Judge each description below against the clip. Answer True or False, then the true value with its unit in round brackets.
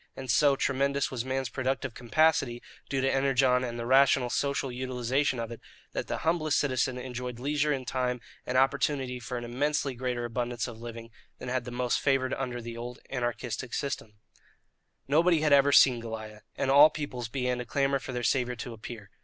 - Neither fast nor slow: True (185 wpm)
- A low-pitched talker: True (130 Hz)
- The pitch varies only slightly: True (2.2 semitones)